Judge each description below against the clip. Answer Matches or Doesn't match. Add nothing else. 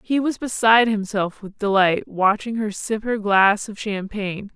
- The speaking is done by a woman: Matches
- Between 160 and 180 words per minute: Matches